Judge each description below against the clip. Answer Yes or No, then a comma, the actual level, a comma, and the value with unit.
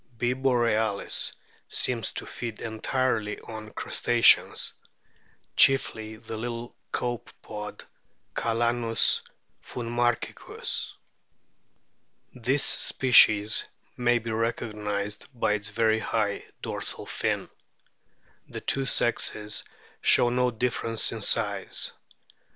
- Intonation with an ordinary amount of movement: No, narrow, 2.0 semitones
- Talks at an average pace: No, slow, 90 wpm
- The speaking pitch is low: Yes, low, 115 Hz